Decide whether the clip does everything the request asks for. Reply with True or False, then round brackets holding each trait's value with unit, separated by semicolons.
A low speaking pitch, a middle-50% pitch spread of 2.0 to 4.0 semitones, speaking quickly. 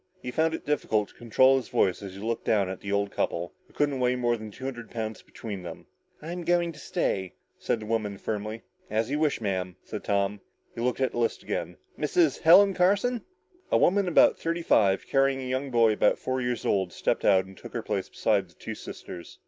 False (115 Hz; 5.4 semitones; 220 wpm)